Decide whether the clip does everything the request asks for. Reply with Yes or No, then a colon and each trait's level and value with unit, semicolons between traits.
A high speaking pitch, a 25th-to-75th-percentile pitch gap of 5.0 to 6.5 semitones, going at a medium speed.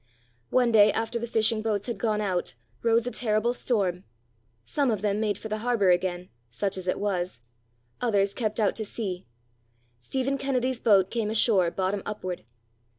No: high, 215 Hz; average, 3.5 semitones; average, 170 wpm